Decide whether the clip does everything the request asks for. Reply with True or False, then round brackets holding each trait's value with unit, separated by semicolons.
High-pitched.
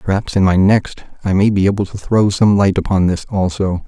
False (95 Hz)